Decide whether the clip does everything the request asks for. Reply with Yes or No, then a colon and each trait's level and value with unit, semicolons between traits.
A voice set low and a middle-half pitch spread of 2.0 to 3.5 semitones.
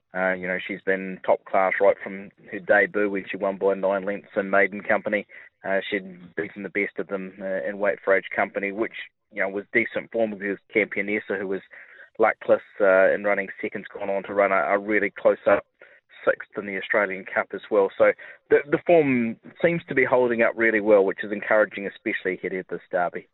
Yes: low, 100 Hz; average, 3.0 semitones